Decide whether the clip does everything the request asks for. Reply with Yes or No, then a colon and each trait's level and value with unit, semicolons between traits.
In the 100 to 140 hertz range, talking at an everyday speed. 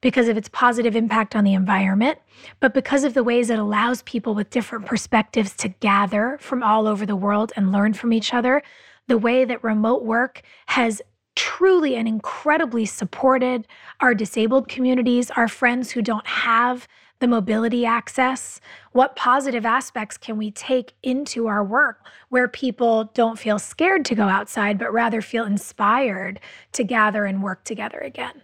No: high, 235 Hz; average, 165 wpm